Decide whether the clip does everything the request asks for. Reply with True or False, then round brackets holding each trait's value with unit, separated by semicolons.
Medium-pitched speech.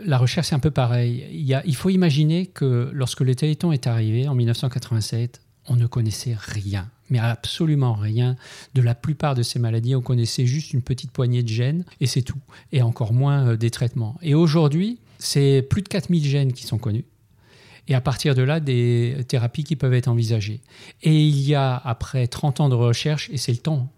False (130 Hz)